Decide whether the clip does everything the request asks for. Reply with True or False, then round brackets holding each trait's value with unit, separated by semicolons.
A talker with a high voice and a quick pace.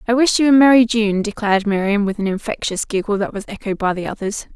True (215 Hz; 235 wpm)